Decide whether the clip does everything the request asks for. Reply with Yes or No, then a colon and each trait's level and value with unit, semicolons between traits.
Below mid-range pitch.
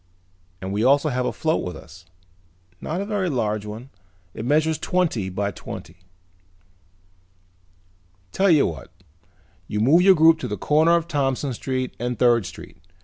Yes: low, 130 Hz